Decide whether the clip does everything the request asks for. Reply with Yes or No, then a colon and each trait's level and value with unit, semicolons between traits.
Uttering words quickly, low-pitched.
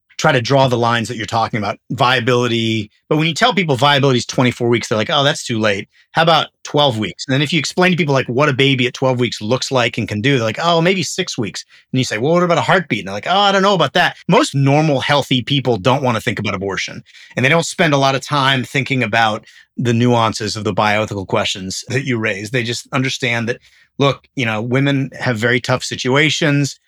Yes: fast, 250 wpm; low, 130 Hz